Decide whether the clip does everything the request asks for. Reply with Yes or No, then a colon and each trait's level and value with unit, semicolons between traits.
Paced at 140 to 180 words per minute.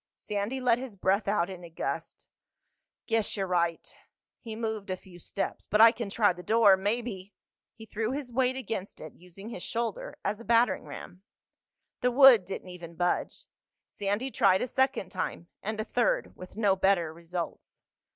Yes: average, 175 wpm